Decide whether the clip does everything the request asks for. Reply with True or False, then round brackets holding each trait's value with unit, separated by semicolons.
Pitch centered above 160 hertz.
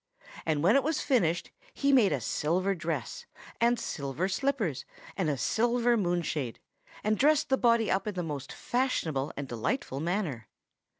True (185 Hz)